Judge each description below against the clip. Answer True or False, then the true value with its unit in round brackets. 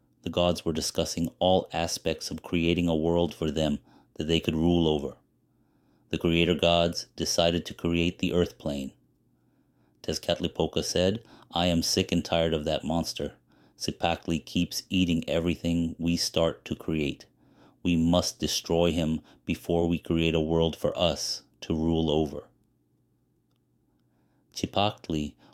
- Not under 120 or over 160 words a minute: True (140 wpm)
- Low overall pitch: True (85 Hz)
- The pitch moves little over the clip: True (1.3 semitones)